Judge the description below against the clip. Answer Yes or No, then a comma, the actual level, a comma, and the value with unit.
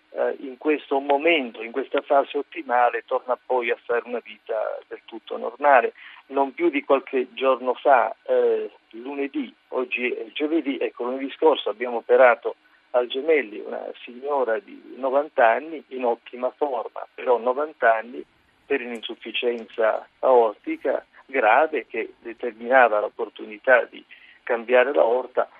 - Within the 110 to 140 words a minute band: Yes, average, 130 wpm